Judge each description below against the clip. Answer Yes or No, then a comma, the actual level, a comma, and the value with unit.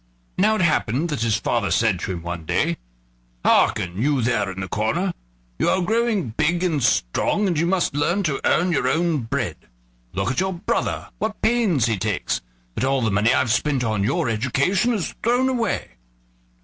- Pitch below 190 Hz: Yes, medium, 140 Hz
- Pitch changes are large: Yes, wide, 8.8 semitones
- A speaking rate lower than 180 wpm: No, average, 190 wpm